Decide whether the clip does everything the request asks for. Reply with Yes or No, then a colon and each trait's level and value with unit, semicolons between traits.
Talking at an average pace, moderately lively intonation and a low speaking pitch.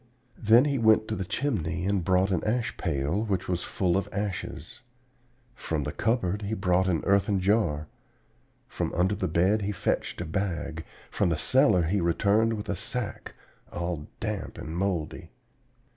Yes: average, 165 wpm; average, 3.8 semitones; very low, 95 Hz